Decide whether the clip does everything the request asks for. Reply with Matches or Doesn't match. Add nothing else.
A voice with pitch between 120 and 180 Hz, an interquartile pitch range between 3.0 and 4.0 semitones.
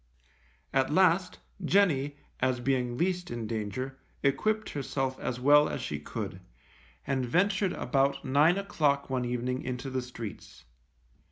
Doesn't match